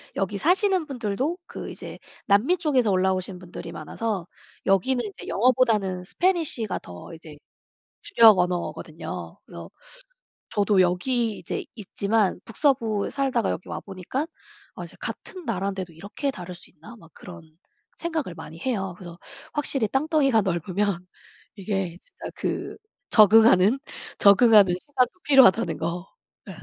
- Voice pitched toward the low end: No, high, 205 Hz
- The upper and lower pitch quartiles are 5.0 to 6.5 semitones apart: Yes, wide, 5.9 semitones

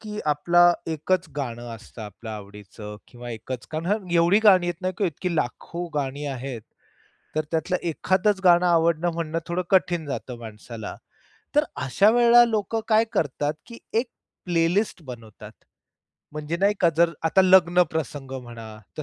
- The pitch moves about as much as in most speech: No, wide, 6.4 semitones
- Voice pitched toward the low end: No, medium, 165 Hz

